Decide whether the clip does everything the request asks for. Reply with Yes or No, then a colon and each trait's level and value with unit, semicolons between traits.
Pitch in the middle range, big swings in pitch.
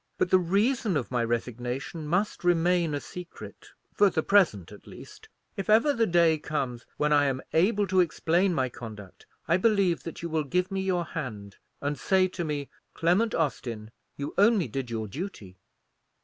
Yes: medium, 165 Hz; wide, 6.3 semitones